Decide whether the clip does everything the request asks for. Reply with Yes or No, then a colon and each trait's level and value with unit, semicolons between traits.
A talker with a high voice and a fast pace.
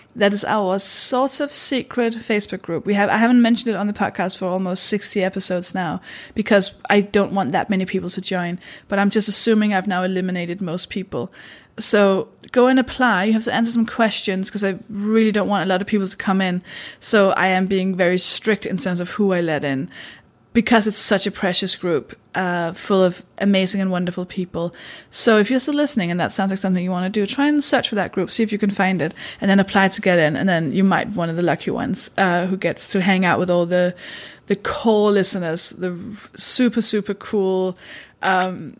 Yes: high, 195 Hz; fast, 225 wpm